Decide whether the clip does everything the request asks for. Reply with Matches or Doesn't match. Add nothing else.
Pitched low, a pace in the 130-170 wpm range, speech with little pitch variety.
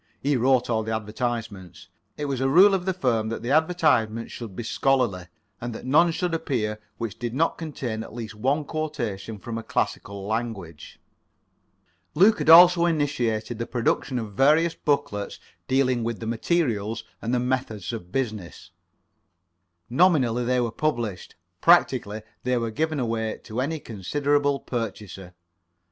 Doesn't match